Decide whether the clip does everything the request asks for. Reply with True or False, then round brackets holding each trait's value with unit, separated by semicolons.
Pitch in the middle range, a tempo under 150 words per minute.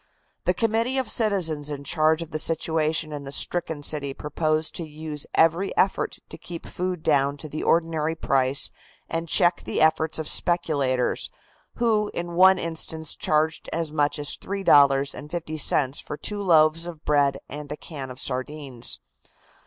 False (155 Hz; 155 wpm)